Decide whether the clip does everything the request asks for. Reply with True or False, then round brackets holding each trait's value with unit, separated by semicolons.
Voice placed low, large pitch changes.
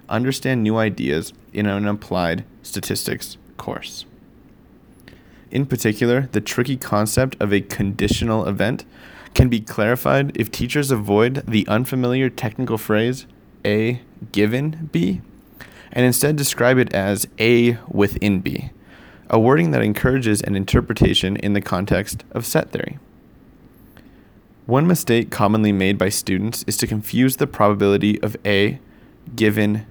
False (110 Hz; 3.5 semitones)